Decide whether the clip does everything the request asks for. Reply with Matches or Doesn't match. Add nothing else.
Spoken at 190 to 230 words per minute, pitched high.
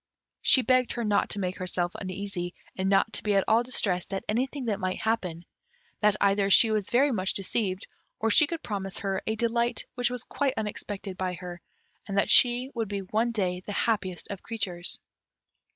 Matches